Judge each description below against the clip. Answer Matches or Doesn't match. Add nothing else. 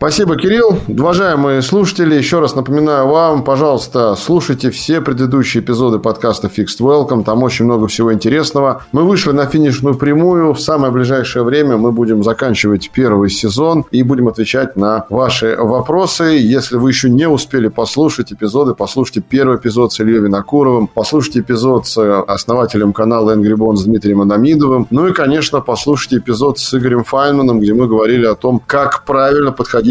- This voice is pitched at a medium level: Doesn't match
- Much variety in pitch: Doesn't match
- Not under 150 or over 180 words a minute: Matches